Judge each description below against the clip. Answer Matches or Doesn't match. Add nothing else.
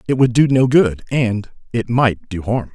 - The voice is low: Matches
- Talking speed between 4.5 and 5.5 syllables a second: Doesn't match